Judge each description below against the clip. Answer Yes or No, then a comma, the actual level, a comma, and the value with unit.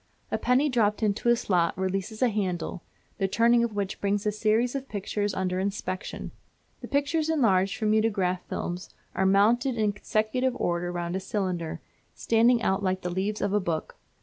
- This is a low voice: No, high, 205 Hz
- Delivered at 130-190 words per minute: Yes, average, 175 wpm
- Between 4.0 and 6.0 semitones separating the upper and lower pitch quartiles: No, average, 3.5 semitones